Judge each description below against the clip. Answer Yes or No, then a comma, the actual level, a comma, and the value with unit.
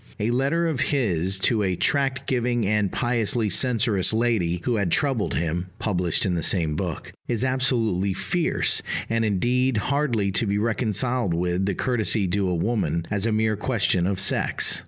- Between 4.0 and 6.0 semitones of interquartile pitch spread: Yes, average, 4.7 semitones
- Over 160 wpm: Yes, average, 175 wpm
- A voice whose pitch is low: Yes, low, 110 Hz